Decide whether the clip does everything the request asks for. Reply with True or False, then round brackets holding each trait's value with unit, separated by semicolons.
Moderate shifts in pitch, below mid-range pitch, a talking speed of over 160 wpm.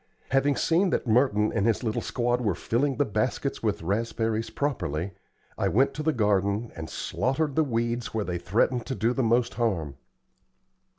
True (4.2 semitones; 115 Hz; 175 wpm)